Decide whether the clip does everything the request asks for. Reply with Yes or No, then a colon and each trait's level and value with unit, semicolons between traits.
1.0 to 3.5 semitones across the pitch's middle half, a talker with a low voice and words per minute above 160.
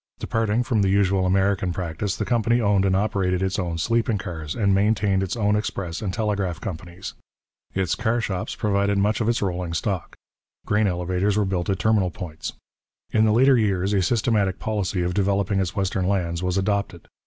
Yes: narrow, 2.5 semitones; low, 100 Hz; average, 185 wpm